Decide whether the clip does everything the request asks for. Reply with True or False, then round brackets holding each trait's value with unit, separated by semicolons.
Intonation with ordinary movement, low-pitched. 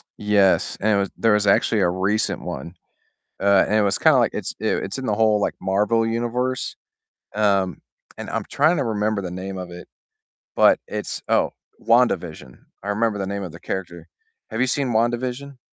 True (3.3 semitones; 105 Hz)